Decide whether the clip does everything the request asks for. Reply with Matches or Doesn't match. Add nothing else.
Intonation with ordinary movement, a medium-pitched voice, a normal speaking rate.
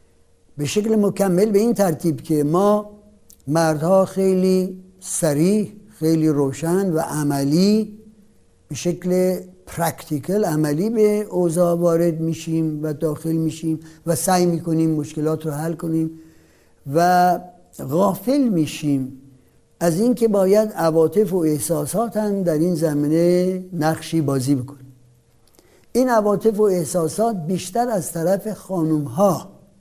Matches